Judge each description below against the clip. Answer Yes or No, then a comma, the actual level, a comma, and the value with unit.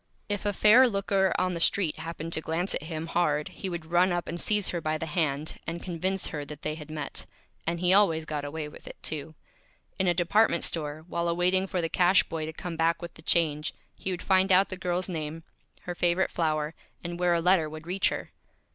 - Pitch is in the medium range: Yes, medium, 170 Hz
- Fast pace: Yes, fast, 225 wpm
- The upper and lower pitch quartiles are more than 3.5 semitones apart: No, narrow, 2.6 semitones